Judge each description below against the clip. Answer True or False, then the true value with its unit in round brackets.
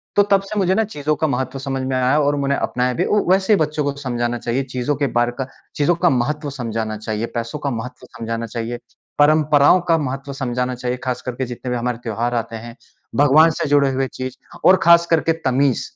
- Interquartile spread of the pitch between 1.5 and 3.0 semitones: False (3.6 semitones)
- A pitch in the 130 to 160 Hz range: True (135 Hz)